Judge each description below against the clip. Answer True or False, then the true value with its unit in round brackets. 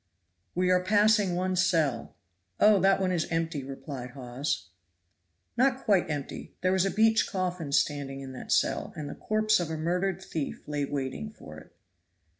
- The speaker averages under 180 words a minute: True (170 wpm)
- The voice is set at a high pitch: False (175 Hz)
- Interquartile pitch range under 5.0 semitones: False (5.3 semitones)